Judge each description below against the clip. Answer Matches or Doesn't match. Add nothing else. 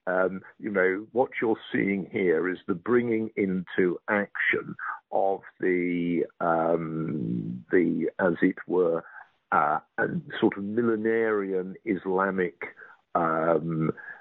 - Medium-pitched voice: Doesn't match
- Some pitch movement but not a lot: Matches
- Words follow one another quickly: Doesn't match